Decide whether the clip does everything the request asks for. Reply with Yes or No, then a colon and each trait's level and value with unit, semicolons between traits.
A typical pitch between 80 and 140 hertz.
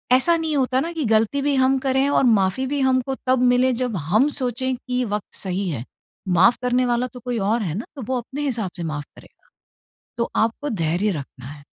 No: very high, 250 Hz